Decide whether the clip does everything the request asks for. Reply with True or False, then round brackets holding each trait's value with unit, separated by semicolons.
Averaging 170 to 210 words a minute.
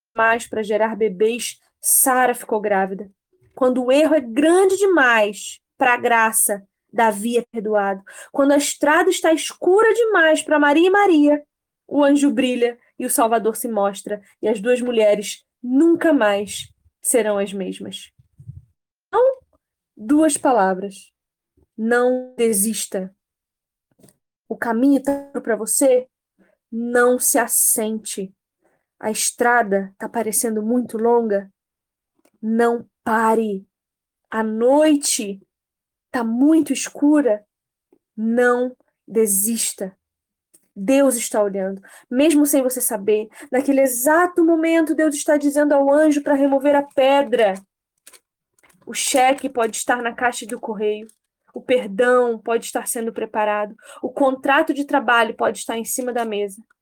False (125 wpm)